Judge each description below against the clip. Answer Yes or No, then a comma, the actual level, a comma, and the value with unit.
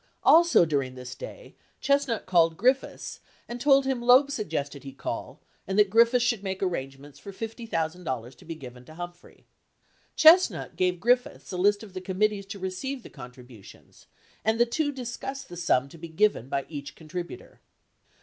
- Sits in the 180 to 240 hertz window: Yes, medium, 185 Hz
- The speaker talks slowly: No, average, 175 wpm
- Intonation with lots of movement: Yes, wide, 7.8 semitones